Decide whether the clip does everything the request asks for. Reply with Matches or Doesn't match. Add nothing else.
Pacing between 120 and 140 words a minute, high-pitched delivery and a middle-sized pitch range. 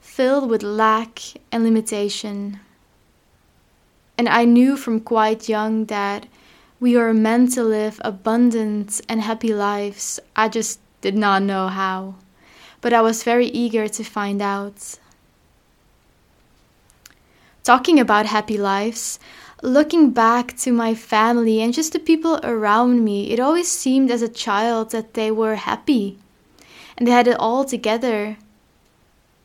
Doesn't match